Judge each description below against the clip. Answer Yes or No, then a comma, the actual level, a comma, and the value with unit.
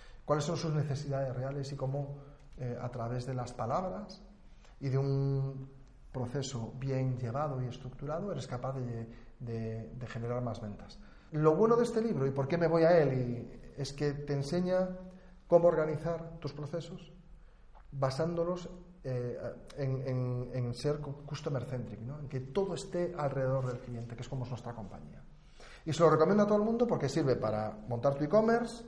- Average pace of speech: Yes, average, 175 wpm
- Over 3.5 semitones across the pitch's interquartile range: Yes, average, 4.9 semitones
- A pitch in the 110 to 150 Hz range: Yes, medium, 140 Hz